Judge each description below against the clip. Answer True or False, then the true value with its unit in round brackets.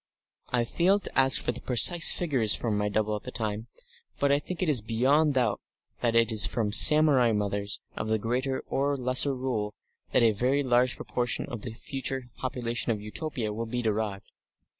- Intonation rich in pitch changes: False (3.6 semitones)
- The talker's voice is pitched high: False (120 Hz)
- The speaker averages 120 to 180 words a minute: False (190 wpm)